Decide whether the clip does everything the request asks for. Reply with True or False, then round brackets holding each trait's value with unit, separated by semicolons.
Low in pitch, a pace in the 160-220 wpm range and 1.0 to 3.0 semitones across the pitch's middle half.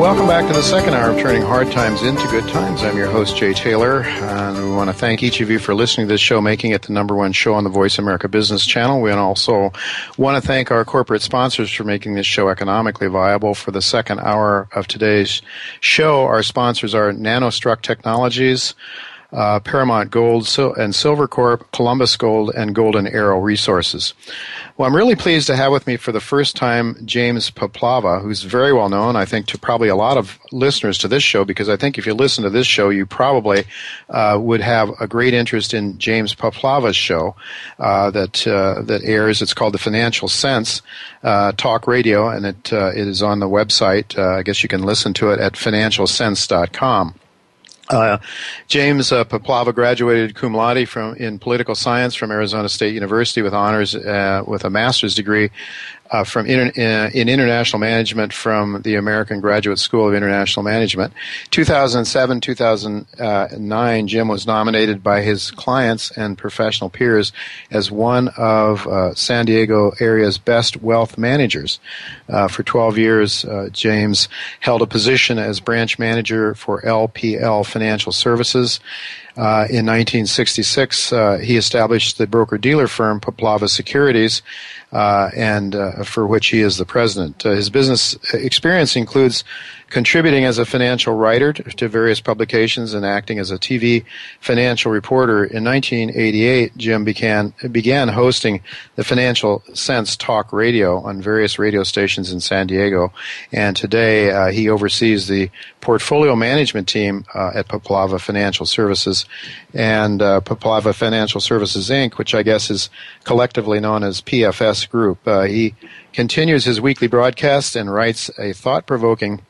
True (110 Hz; 170 wpm; 2.7 semitones)